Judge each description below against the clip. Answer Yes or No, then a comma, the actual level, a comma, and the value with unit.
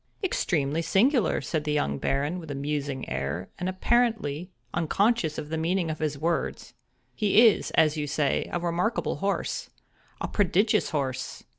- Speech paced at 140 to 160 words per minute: Yes, average, 150 wpm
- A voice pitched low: No, medium, 160 Hz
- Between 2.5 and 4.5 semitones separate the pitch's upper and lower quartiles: No, average, 5.0 semitones